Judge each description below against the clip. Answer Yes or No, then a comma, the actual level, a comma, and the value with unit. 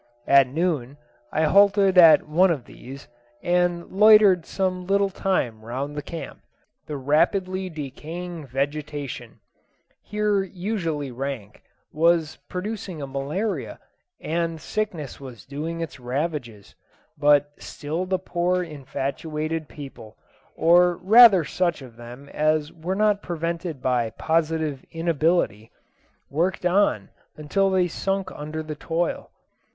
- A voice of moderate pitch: Yes, medium, 160 Hz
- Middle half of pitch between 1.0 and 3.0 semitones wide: No, average, 4.4 semitones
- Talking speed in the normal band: No, slow, 120 wpm